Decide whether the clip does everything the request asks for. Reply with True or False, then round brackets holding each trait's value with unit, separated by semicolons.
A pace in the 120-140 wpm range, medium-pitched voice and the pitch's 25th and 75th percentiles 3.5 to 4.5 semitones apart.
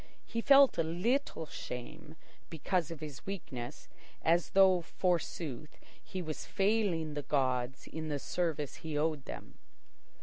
True (135 wpm; 160 Hz; 3.8 semitones)